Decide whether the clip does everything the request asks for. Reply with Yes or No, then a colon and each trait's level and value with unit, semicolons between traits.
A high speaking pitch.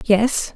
Yes: high, 225 Hz